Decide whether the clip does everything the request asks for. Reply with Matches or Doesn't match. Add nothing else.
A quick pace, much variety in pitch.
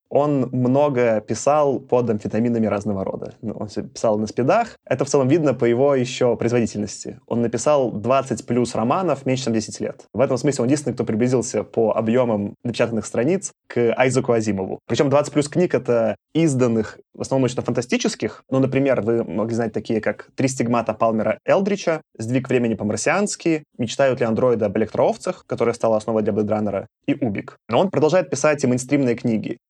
Doesn't match